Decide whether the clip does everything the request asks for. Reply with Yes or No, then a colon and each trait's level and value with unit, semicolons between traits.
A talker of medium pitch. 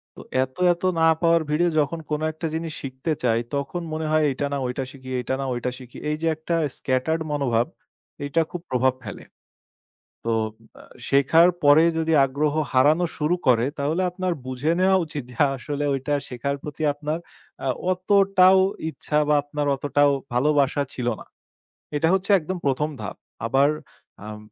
Yes: medium, 145 Hz